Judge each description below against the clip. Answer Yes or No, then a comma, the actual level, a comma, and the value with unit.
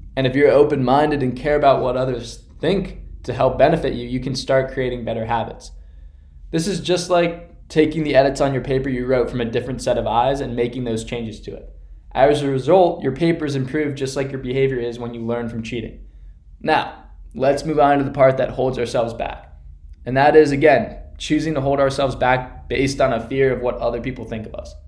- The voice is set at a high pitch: No, low, 130 Hz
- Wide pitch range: No, average, 3.0 semitones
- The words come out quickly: Yes, fast, 220 wpm